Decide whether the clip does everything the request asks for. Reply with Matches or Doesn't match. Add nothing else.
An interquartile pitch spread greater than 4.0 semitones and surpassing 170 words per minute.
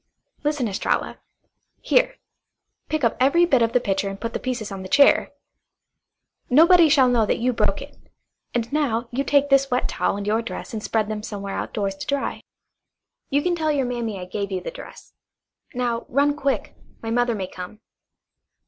Matches